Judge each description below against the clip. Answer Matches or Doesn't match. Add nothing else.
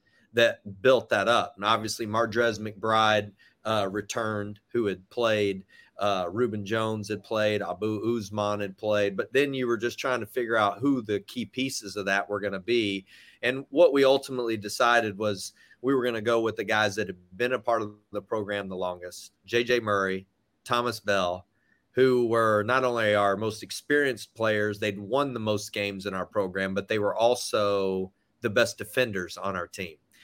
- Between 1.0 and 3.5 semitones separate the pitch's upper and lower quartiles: Matches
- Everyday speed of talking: Matches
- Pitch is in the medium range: Doesn't match